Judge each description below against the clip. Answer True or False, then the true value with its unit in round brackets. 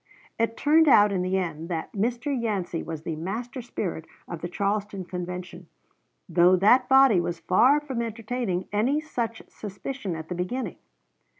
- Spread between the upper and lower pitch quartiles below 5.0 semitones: False (5.5 semitones)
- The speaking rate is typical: True (160 wpm)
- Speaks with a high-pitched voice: True (200 Hz)